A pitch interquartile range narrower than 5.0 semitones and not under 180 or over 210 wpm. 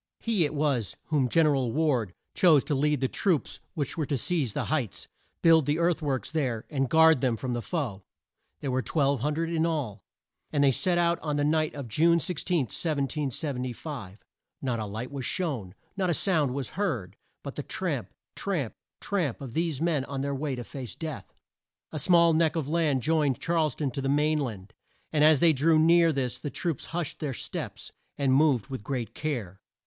Yes: average, 3.8 semitones; average, 195 wpm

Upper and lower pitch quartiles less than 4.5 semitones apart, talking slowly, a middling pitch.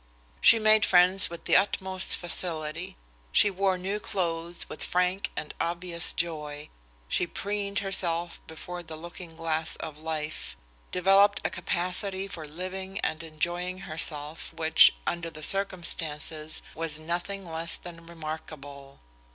Yes: average, 2.8 semitones; slow, 130 wpm; medium, 170 Hz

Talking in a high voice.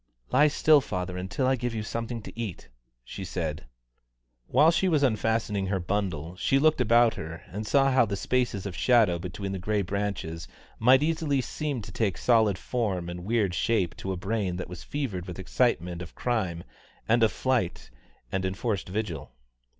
No: low, 105 Hz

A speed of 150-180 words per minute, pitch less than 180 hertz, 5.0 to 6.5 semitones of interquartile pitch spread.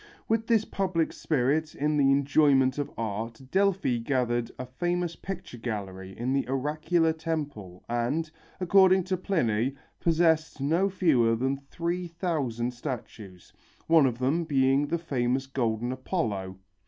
No: slow, 135 wpm; medium, 140 Hz; wide, 5.6 semitones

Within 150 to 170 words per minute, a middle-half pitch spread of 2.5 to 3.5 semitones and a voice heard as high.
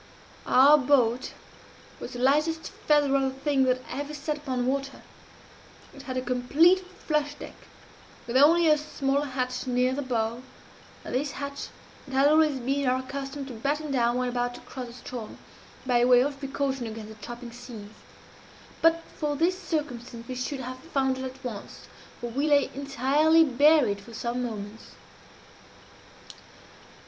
Yes: average, 160 wpm; average, 2.9 semitones; very high, 265 Hz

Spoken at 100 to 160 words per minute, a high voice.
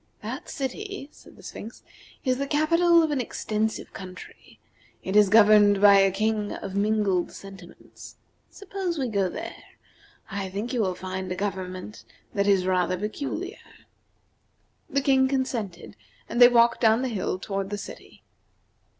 Yes: average, 150 wpm; high, 210 Hz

